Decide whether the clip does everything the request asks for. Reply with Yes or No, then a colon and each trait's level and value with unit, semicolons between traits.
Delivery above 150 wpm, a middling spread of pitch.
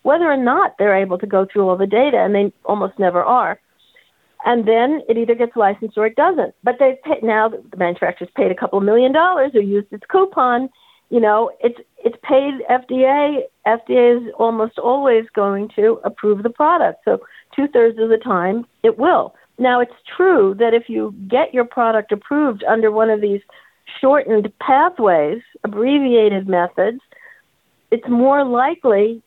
Yes: average, 170 wpm; average, 3.9 semitones